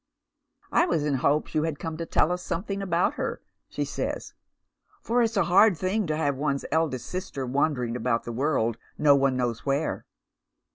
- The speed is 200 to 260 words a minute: Yes, fast, 205 wpm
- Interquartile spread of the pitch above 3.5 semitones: Yes, average, 4.9 semitones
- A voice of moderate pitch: Yes, medium, 150 Hz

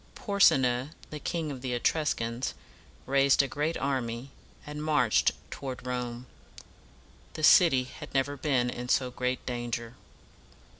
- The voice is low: Yes, low, 130 Hz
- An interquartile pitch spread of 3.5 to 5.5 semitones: No, average, 3.0 semitones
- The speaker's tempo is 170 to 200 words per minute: No, average, 145 wpm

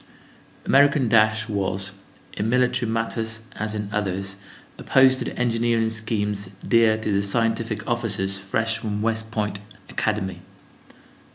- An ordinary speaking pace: No, slow, 125 wpm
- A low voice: Yes, low, 110 Hz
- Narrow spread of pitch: Yes, narrow, 2.0 semitones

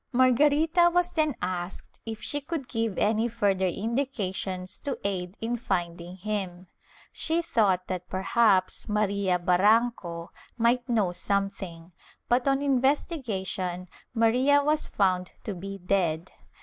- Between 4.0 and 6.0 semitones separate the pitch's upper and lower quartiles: Yes, wide, 5.4 semitones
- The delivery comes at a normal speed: No, slow, 125 wpm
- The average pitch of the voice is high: Yes, high, 210 Hz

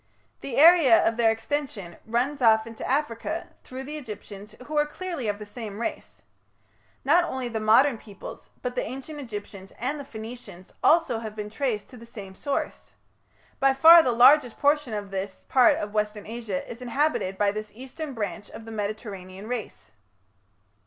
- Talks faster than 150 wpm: Yes, average, 175 wpm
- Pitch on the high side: Yes, high, 230 Hz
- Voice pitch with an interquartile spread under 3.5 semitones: No, average, 4.5 semitones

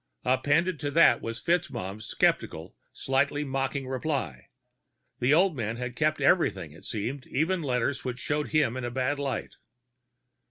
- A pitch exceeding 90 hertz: Yes, low, 135 Hz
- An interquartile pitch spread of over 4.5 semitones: No, average, 3.6 semitones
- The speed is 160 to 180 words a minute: No, average, 150 wpm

